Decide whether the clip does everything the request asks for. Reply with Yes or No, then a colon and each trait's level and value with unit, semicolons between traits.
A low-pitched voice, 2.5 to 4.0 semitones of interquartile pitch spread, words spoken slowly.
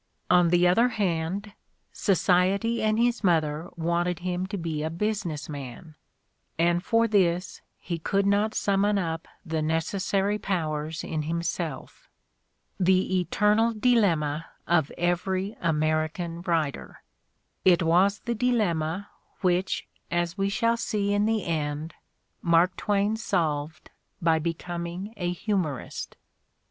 No: medium, 175 Hz; average, 3.7 semitones; slow, 120 wpm